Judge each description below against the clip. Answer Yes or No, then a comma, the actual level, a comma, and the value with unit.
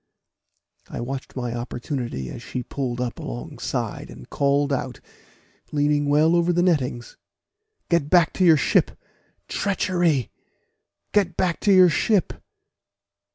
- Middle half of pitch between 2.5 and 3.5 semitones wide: No, wide, 5.6 semitones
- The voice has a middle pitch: Yes, medium, 145 Hz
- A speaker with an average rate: No, slow, 125 wpm